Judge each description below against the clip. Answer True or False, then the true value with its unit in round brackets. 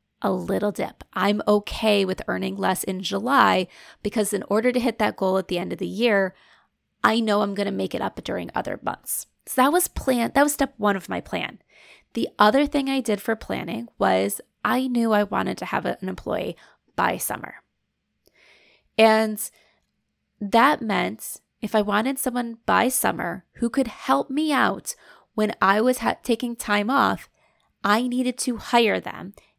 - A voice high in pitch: True (220 Hz)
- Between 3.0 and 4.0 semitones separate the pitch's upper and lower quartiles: True (3.6 semitones)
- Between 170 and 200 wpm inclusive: True (180 wpm)